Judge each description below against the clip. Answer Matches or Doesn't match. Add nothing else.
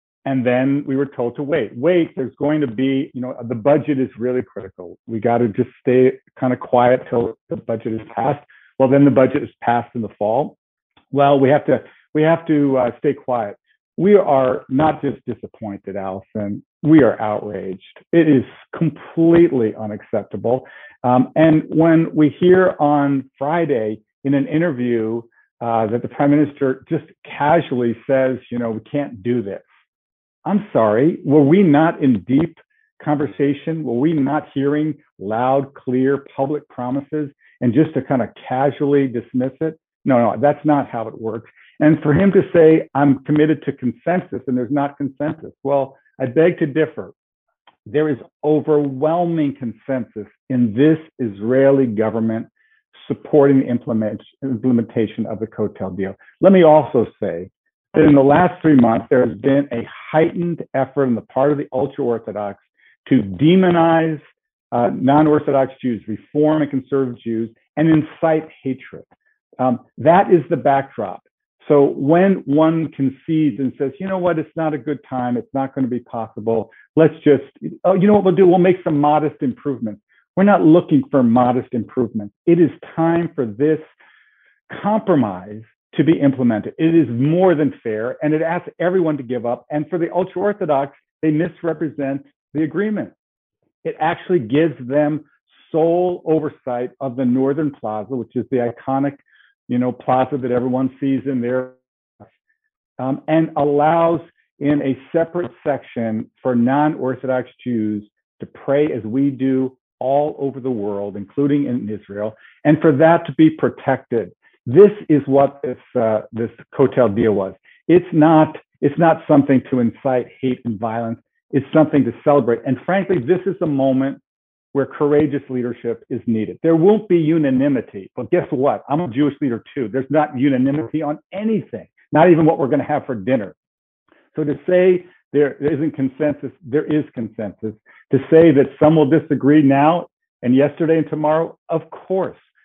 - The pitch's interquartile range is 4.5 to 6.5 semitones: Doesn't match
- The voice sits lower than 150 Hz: Matches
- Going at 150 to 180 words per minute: Matches